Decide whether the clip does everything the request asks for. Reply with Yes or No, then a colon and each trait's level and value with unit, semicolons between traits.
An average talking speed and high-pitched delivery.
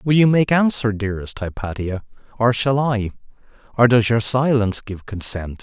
No: average, 150 wpm; low, 115 Hz